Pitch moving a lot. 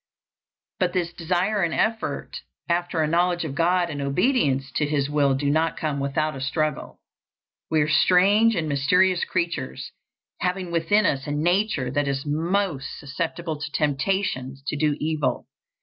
No: average, 3.9 semitones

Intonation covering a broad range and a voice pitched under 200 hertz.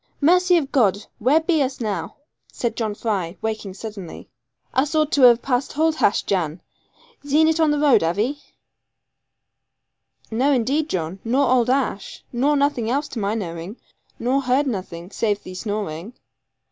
No: wide, 5.9 semitones; high, 240 Hz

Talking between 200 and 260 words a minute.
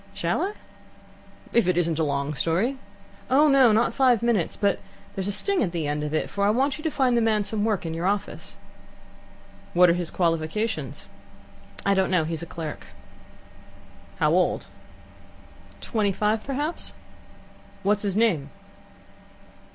No: average, 160 wpm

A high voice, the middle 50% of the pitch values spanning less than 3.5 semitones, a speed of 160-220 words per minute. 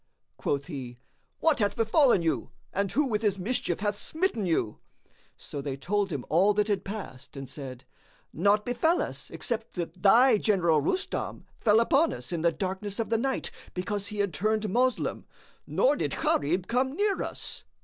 No: high, 205 Hz; wide, 5.4 semitones; average, 175 wpm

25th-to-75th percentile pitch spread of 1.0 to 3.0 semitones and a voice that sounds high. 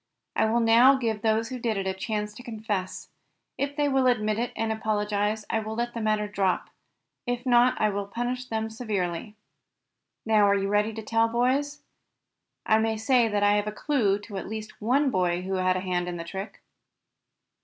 Yes: average, 2.7 semitones; high, 220 Hz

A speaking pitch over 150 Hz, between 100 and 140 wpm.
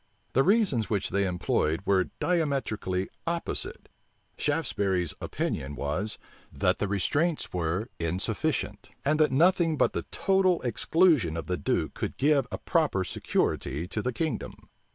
No: low, 115 Hz; slow, 135 wpm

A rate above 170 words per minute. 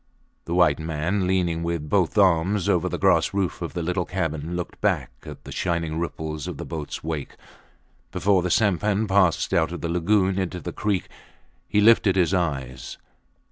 Yes: average, 180 wpm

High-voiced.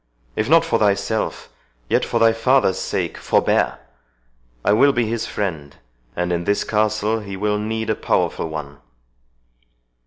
No: low, 105 Hz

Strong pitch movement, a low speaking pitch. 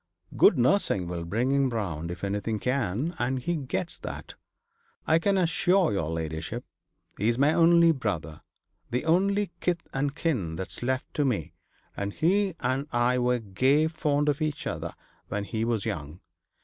Yes: wide, 7.9 semitones; low, 125 Hz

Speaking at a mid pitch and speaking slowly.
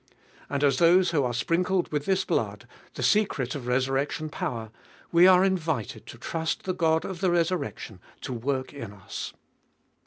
No: medium, 155 Hz; average, 175 wpm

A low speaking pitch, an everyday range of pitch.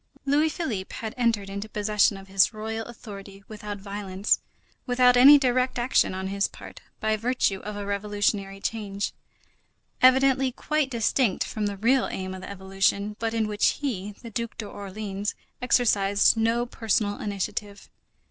No: high, 210 Hz; average, 3.1 semitones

